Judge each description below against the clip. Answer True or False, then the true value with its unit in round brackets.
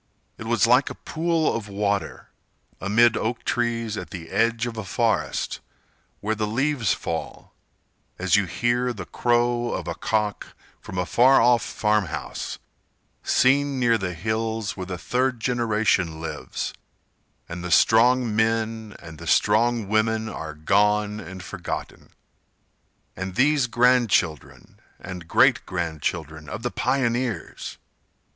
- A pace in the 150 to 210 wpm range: False (140 wpm)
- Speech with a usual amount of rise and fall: True (4.0 semitones)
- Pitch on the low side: True (110 Hz)